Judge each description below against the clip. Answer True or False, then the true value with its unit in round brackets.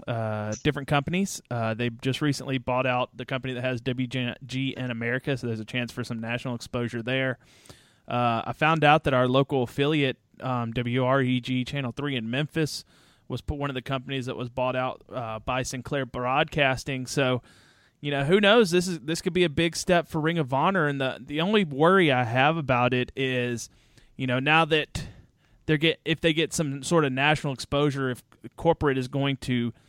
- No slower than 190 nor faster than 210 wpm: True (195 wpm)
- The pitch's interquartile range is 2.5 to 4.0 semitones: True (3.2 semitones)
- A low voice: True (130 Hz)